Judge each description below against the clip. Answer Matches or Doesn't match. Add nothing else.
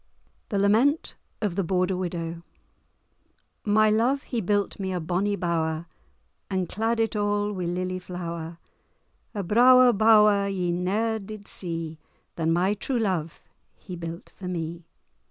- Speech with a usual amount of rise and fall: Matches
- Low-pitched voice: Doesn't match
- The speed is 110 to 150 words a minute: Matches